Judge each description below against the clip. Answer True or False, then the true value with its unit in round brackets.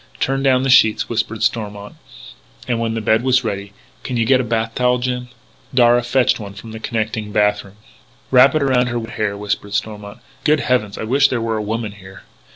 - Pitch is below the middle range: True (115 Hz)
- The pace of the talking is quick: True (210 wpm)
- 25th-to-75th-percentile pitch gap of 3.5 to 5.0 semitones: False (3.0 semitones)